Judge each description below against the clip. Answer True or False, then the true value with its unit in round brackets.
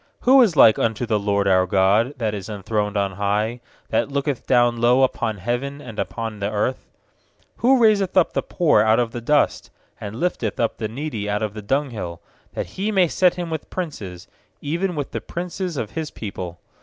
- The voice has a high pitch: False (120 Hz)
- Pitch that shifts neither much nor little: False (6.7 semitones)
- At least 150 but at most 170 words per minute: False (195 wpm)